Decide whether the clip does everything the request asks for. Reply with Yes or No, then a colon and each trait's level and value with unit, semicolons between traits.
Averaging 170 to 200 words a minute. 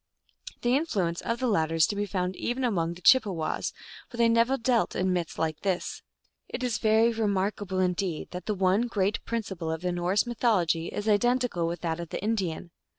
Yes: average, 195 wpm